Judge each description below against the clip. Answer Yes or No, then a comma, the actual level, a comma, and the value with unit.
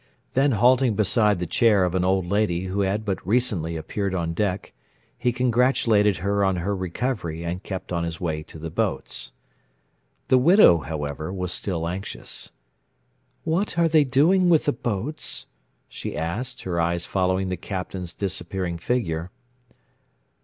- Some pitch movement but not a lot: No, wide, 5.8 semitones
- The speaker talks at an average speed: Yes, average, 155 wpm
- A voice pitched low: Yes, very low, 95 Hz